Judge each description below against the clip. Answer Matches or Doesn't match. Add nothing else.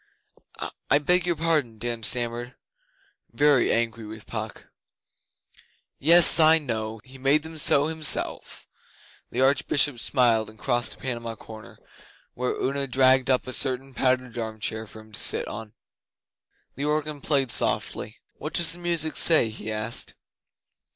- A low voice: Matches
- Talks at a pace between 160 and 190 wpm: Doesn't match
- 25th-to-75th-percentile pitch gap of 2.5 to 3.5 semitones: Doesn't match